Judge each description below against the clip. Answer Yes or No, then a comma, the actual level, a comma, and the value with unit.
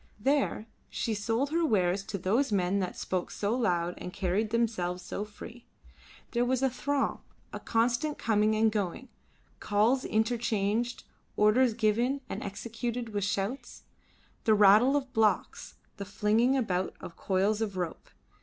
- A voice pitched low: No, high, 220 Hz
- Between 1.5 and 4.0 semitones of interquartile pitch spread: Yes, average, 3.4 semitones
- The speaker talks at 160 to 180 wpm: No, average, 145 wpm